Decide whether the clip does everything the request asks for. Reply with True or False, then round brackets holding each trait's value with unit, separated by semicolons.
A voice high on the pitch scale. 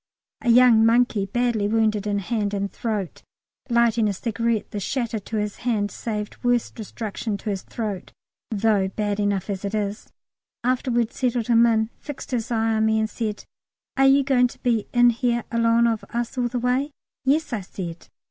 True (225 Hz)